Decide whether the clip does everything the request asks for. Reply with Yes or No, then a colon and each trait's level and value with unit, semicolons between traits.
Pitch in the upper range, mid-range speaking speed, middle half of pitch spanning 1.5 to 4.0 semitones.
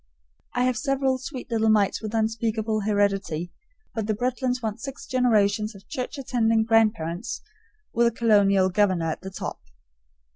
Yes: high, 220 Hz; average, 150 wpm; average, 3.3 semitones